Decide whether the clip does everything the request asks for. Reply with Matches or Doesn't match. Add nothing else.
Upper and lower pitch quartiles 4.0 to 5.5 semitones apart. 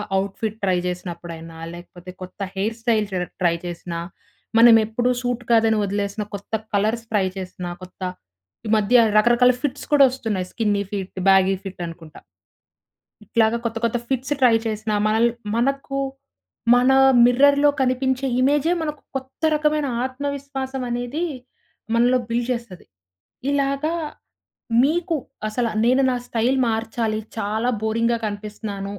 Matches